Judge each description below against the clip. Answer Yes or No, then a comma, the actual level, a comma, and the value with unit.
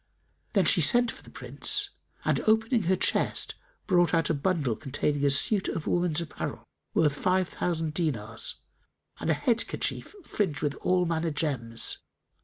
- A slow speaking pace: No, average, 160 wpm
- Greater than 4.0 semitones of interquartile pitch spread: Yes, average, 4.4 semitones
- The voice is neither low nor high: Yes, medium, 165 Hz